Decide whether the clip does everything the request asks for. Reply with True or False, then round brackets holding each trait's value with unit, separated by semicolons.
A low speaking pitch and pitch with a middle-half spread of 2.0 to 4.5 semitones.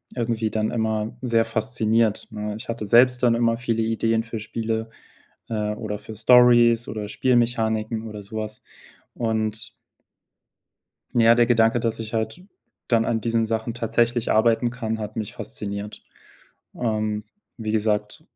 False (115 Hz; 1.3 semitones)